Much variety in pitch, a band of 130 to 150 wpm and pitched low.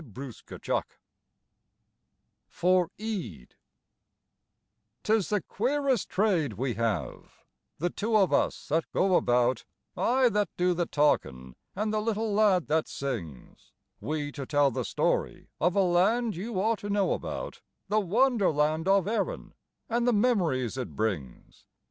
No: wide, 7.5 semitones; average, 140 wpm; medium, 180 Hz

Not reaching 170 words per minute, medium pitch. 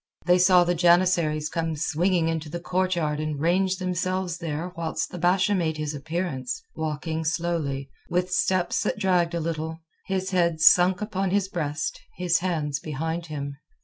Yes: average, 160 wpm; medium, 170 Hz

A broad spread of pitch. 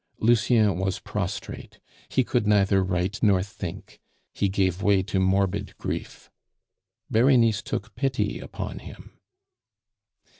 No: narrow, 2.6 semitones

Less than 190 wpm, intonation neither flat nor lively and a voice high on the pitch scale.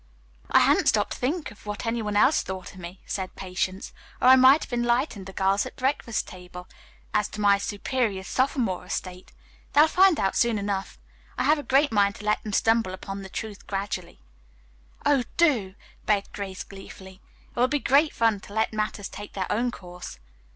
No: average, 195 wpm; average, 4.4 semitones; high, 205 Hz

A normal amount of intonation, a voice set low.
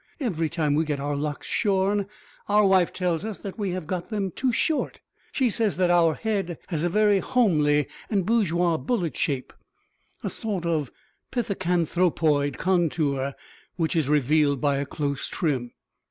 No: average, 5.0 semitones; medium, 175 Hz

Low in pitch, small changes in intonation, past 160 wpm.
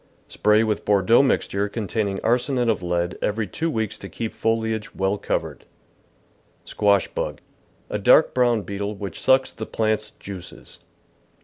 No: low, 105 Hz; narrow, 2.1 semitones; average, 145 wpm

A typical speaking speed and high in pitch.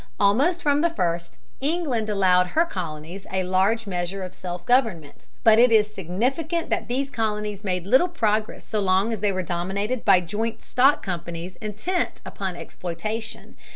Yes: average, 160 wpm; high, 210 Hz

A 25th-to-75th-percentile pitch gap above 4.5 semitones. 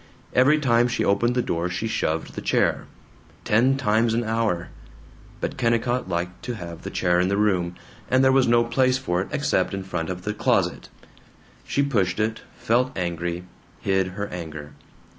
Yes: average, 5.3 semitones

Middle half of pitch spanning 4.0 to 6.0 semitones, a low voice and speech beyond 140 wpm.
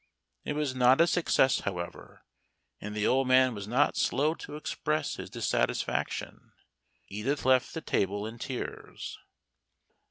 No: wide, 5.5 semitones; low, 130 Hz; slow, 135 wpm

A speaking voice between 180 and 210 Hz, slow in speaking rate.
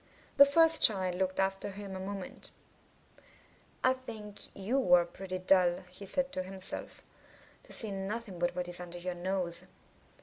No: high, 190 Hz; average, 160 wpm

